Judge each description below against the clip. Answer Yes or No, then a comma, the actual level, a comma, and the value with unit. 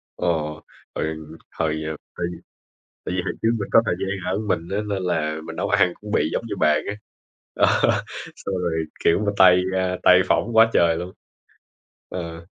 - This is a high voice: No, very low, 90 Hz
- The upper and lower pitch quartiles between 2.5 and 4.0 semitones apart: Yes, average, 3.0 semitones